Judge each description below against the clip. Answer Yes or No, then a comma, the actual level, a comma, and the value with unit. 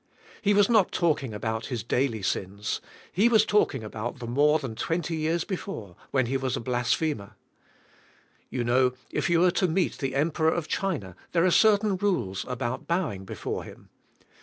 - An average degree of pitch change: No, wide, 7.0 semitones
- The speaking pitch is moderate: Yes, medium, 145 Hz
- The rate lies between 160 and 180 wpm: Yes, average, 175 wpm